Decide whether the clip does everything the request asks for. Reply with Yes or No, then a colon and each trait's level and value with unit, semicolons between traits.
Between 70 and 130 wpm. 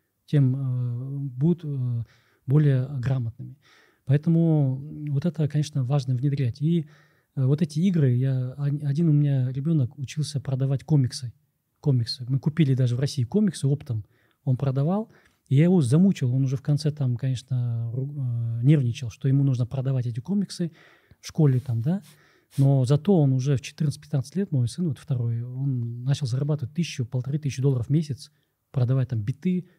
No: fast, 160 wpm